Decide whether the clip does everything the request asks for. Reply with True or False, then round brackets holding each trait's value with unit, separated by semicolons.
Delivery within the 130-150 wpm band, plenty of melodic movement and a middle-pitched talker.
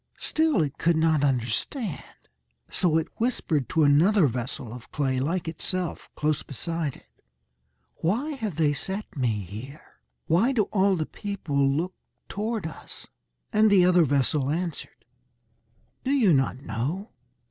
True (140 wpm; 5.9 semitones; 160 Hz)